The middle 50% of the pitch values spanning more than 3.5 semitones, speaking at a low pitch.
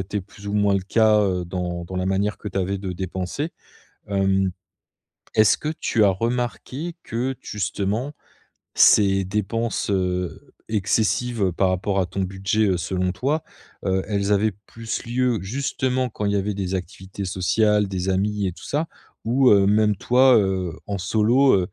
No: average, 3.0 semitones; low, 100 Hz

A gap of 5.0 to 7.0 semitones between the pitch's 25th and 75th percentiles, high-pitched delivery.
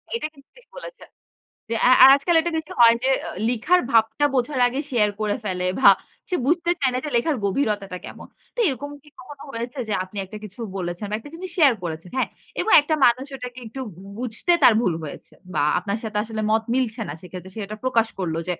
Yes: average, 5.3 semitones; high, 235 Hz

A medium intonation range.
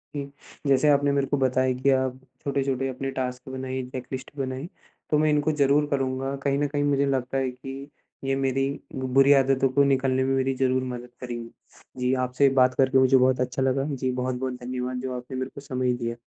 No: narrow, 1.2 semitones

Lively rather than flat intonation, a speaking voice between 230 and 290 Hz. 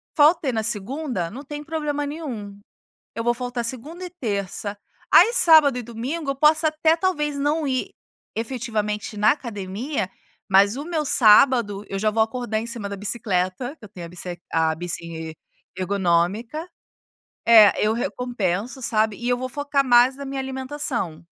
Yes: wide, 5.8 semitones; high, 240 Hz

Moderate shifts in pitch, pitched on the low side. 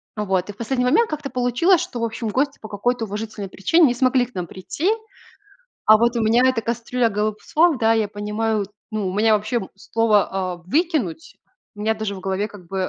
No: average, 3.4 semitones; high, 225 Hz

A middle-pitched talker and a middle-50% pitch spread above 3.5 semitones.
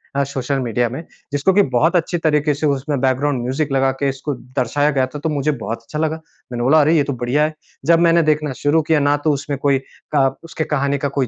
No: medium, 145 Hz; narrow, 2.5 semitones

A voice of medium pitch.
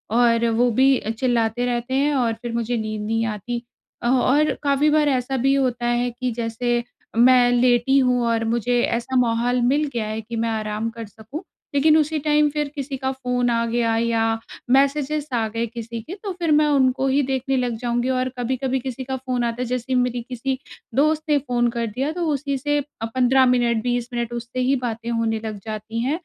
No: high, 245 Hz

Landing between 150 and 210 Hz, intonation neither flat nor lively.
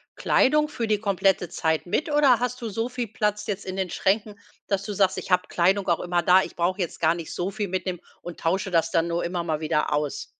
Yes: high, 190 Hz; average, 3.4 semitones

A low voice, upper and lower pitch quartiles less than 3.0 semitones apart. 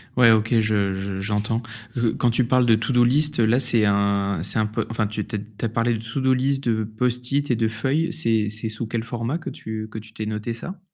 Yes: low, 115 Hz; narrow, 2.4 semitones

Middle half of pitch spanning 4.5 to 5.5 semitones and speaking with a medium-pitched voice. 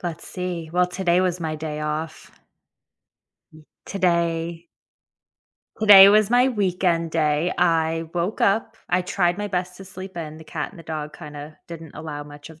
No: average, 2.7 semitones; medium, 170 Hz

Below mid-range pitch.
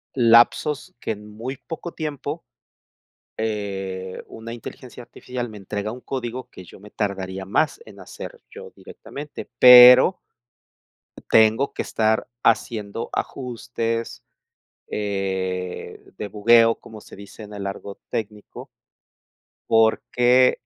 Yes: low, 110 Hz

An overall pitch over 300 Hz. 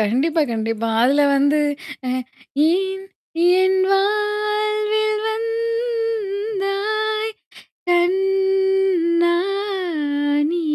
Yes: very high, 385 Hz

